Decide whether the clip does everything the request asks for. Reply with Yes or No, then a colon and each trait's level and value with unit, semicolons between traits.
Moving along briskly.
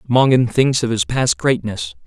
No: average, 175 wpm